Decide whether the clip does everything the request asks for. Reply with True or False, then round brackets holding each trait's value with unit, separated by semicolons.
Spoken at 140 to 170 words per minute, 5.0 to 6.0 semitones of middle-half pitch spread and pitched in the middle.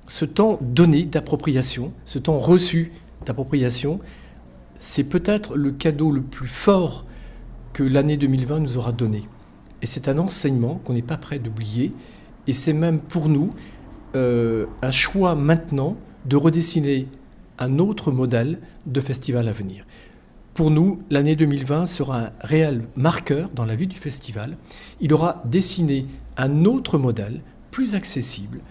False (145 wpm; 4.6 semitones; 145 Hz)